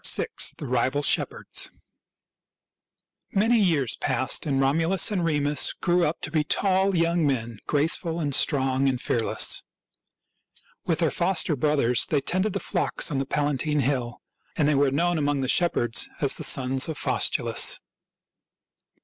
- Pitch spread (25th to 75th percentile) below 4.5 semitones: Yes, average, 3.9 semitones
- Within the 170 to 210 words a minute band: No, average, 150 wpm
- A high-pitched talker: No, medium, 145 Hz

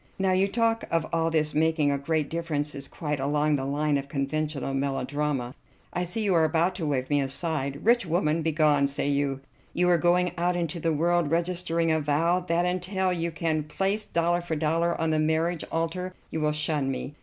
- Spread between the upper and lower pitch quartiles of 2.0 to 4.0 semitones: Yes, average, 2.9 semitones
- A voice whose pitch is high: No, medium, 160 Hz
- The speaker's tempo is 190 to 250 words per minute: Yes, average, 200 wpm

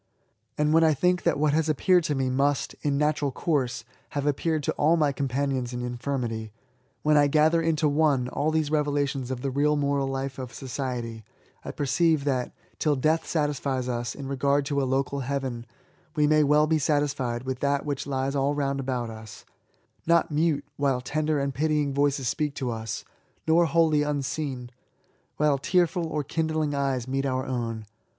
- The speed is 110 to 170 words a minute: No, average, 180 wpm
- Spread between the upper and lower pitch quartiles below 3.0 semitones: Yes, narrow, 2.5 semitones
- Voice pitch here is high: No, medium, 140 Hz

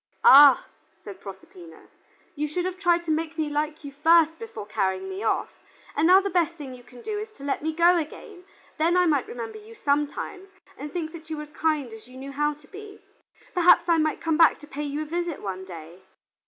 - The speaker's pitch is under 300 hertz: No, very high, 310 Hz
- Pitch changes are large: No, average, 3.8 semitones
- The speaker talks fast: Yes, fast, 225 wpm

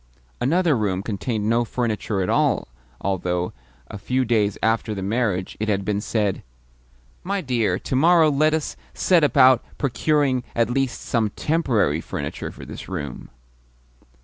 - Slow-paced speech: No, average, 150 wpm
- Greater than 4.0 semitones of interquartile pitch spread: Yes, average, 5.1 semitones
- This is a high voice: No, low, 115 Hz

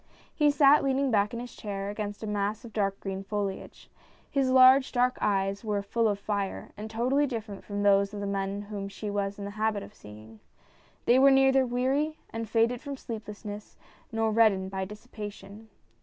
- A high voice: Yes, high, 210 Hz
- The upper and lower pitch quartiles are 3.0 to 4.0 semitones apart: Yes, average, 3.6 semitones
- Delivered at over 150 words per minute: Yes, average, 190 wpm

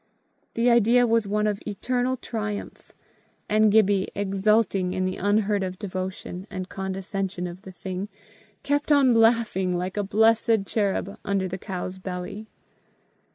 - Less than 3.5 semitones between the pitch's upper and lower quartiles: Yes, average, 2.8 semitones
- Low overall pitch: No, high, 200 Hz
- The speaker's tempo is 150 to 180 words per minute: No, average, 140 wpm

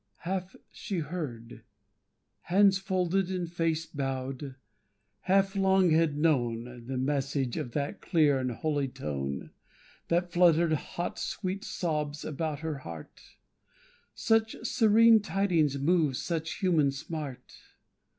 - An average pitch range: Yes, average, 5.0 semitones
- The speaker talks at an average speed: No, slow, 115 wpm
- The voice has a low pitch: No, medium, 160 Hz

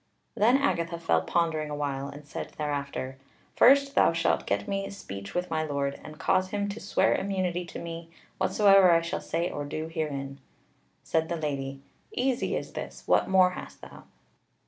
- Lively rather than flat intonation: No, average, 4.5 semitones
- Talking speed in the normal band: Yes, average, 175 wpm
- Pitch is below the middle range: No, medium, 165 Hz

